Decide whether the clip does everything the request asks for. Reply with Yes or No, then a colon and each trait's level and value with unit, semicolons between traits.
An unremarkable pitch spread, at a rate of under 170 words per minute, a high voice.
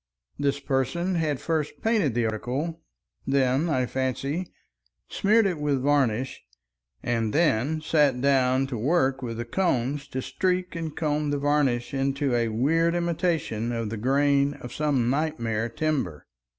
No: average, 4.1 semitones; average, 145 wpm; medium, 140 Hz